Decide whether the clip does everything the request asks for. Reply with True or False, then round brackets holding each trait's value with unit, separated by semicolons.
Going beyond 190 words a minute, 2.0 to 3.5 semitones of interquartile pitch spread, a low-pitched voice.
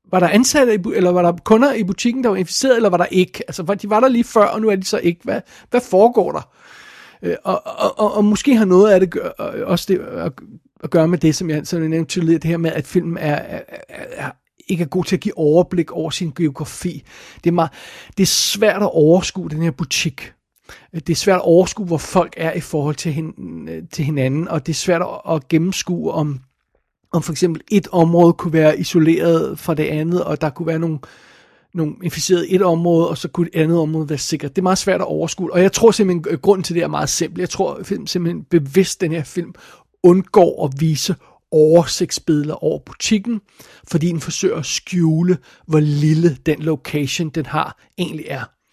False (215 wpm; 2.8 semitones; 170 Hz)